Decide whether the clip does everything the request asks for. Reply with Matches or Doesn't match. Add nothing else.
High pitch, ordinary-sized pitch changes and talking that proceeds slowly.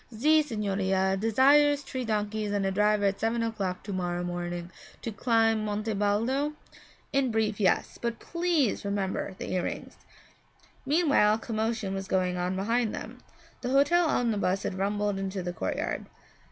Doesn't match